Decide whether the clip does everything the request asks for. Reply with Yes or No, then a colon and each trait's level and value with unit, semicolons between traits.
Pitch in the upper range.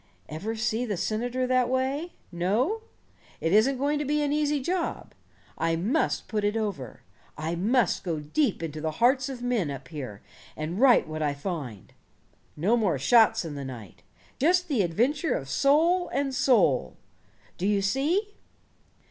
Yes: high, 220 Hz